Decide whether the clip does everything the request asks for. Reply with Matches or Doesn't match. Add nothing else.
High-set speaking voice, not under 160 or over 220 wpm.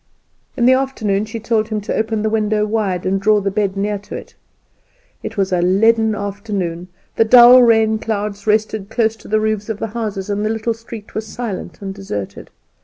Matches